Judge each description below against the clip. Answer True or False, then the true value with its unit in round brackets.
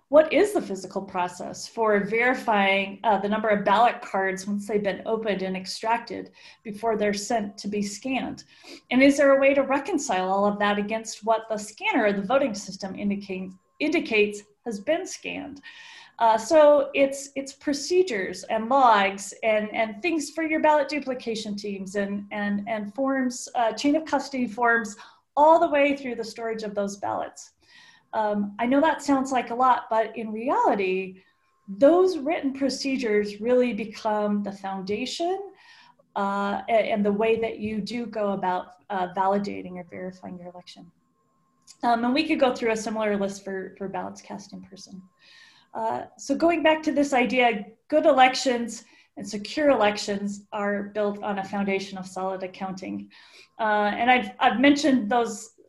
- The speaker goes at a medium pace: True (165 wpm)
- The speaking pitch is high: True (225 Hz)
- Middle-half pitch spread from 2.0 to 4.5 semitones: False (5.2 semitones)